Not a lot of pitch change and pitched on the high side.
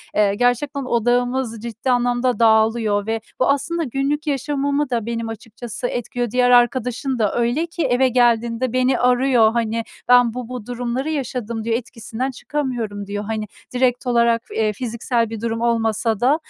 Yes: narrow, 2.2 semitones; high, 240 Hz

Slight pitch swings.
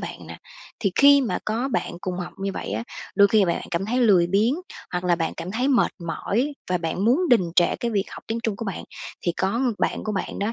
No: average, 4.7 semitones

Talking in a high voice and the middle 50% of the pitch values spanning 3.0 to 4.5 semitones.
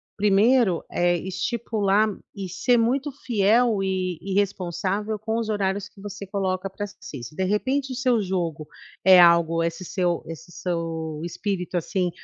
Yes: high, 195 Hz; average, 3.3 semitones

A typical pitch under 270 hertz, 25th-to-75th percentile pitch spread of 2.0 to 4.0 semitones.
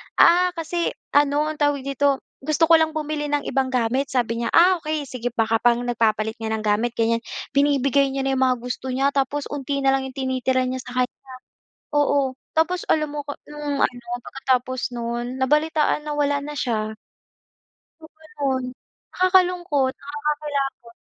No: very high, 275 Hz; average, 3.0 semitones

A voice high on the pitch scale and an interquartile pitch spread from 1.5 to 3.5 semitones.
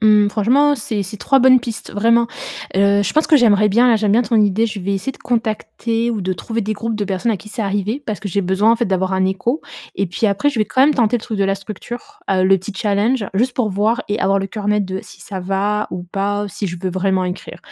Yes: high, 210 Hz; average, 2.9 semitones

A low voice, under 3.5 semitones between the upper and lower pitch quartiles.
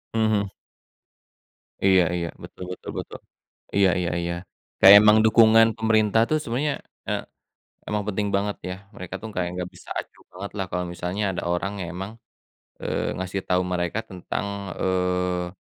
Yes: very low, 95 Hz; average, 2.9 semitones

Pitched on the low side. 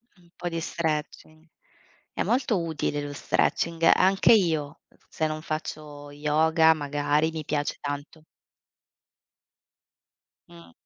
No: medium, 155 Hz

